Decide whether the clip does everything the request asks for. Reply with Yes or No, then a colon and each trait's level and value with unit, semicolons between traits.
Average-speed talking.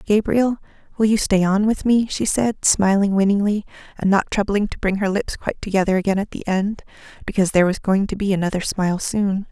No: fast, 210 wpm